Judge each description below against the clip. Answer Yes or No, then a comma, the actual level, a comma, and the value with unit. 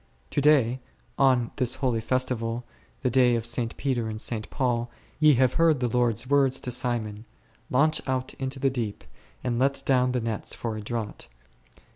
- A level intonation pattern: Yes, narrow, 2.3 semitones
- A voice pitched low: Yes, low, 125 Hz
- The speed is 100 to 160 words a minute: No, average, 180 wpm